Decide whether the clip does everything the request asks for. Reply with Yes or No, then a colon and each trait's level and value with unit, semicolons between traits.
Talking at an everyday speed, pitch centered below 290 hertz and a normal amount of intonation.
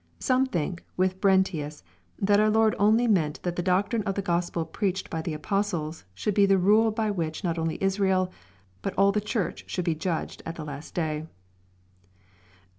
Yes: average, 190 wpm; medium, 185 Hz; average, 3.8 semitones